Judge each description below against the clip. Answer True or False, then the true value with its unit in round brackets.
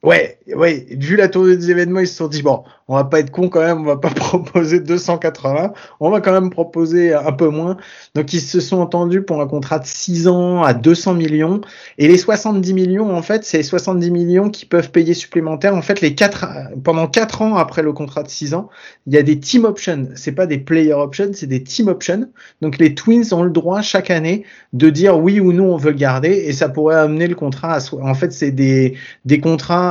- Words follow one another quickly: True (240 wpm)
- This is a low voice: False (170 Hz)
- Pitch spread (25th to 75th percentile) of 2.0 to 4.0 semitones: True (3.3 semitones)